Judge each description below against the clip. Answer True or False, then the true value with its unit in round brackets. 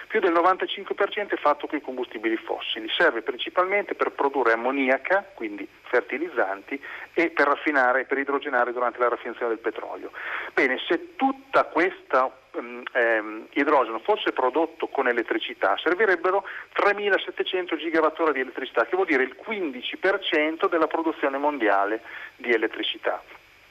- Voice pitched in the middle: True (170 Hz)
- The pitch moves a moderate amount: False (7.8 semitones)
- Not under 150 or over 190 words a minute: False (135 wpm)